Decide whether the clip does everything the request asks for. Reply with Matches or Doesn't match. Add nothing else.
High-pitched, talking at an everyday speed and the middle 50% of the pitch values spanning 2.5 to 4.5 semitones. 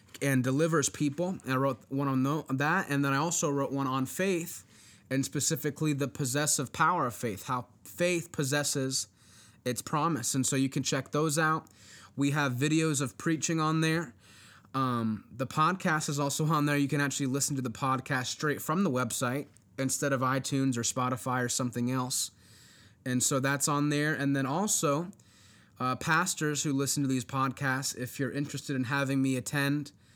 Doesn't match